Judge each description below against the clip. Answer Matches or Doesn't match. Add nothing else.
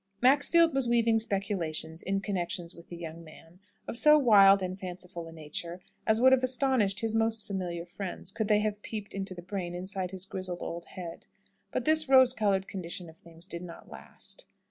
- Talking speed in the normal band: Matches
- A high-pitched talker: Matches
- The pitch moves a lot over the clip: Doesn't match